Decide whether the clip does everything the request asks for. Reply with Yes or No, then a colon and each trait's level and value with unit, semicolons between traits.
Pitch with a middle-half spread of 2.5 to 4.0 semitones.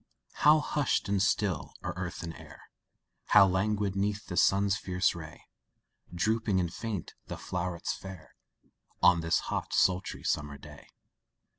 Yes: average, 2.9 semitones